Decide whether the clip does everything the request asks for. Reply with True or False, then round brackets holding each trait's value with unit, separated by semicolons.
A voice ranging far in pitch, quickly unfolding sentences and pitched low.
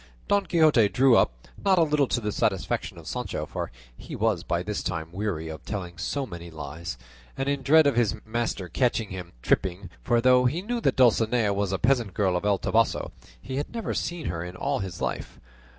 True (7.0 semitones; 210 wpm; 110 Hz)